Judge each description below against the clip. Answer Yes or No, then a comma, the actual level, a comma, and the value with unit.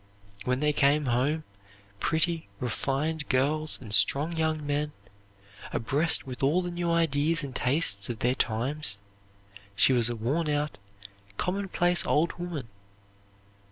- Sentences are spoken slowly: Yes, slow, 130 wpm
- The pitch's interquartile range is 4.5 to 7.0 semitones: No, average, 4.1 semitones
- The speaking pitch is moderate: Yes, medium, 150 Hz